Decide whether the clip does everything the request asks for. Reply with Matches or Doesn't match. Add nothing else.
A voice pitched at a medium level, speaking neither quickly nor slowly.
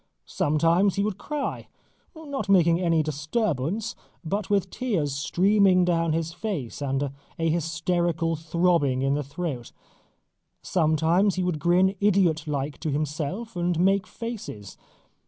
Doesn't match